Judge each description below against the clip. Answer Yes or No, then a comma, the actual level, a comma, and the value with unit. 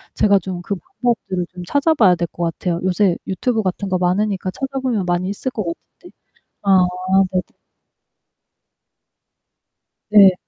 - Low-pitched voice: No, high, 190 Hz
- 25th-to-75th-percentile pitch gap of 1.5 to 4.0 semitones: Yes, average, 3.3 semitones